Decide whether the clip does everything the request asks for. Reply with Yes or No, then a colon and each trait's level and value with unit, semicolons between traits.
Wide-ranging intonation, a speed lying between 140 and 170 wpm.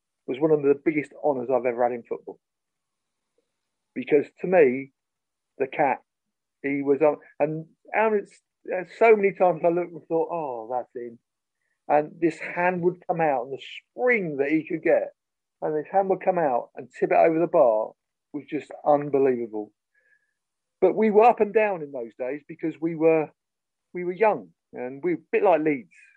No: wide, 6.6 semitones; average, 185 wpm